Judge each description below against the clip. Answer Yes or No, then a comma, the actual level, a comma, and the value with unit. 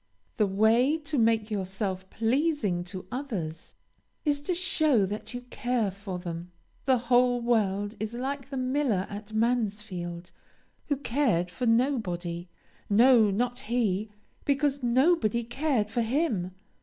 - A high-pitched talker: Yes, high, 230 Hz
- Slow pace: Yes, slow, 130 wpm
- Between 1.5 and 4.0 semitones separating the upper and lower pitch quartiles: No, average, 4.9 semitones